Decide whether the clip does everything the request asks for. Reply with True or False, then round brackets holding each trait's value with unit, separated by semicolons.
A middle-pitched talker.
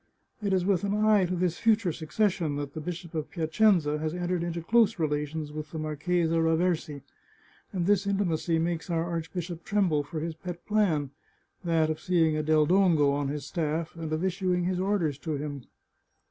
True (165 Hz)